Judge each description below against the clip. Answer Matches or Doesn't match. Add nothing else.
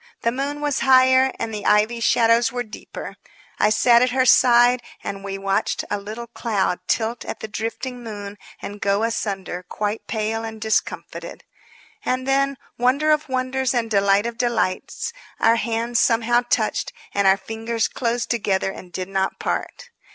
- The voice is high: Matches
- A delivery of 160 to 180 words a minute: Matches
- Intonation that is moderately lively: Matches